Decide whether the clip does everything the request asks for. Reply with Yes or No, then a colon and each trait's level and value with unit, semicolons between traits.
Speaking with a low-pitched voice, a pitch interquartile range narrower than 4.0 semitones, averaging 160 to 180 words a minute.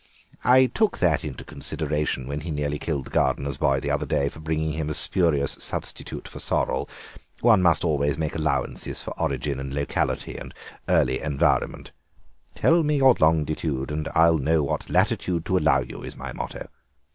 Yes: very low, 75 Hz; average, 2.8 semitones; average, 175 wpm